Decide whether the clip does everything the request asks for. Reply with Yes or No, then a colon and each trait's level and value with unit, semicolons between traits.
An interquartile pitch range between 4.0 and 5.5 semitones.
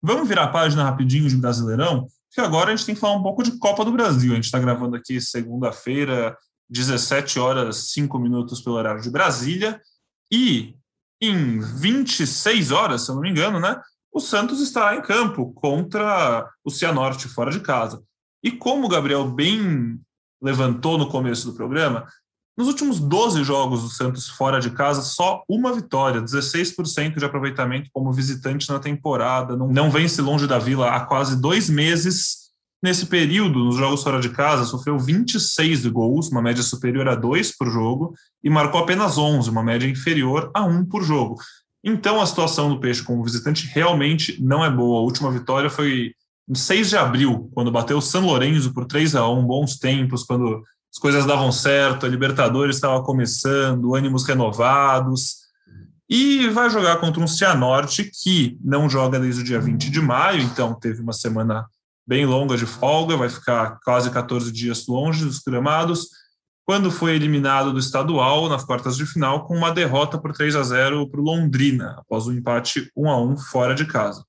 Yes: average, 4.7 semitones